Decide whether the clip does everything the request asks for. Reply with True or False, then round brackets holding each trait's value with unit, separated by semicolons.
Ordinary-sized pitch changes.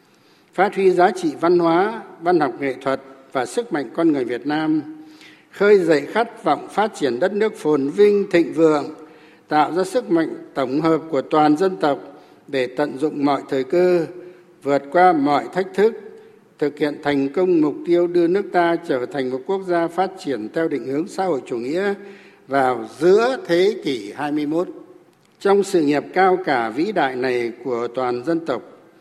False (5.8 semitones)